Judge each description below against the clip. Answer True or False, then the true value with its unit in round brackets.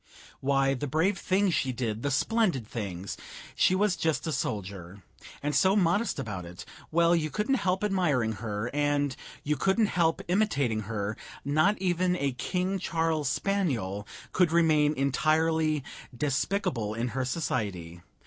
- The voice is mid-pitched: True (150 Hz)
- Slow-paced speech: False (145 wpm)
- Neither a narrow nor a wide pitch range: False (7.5 semitones)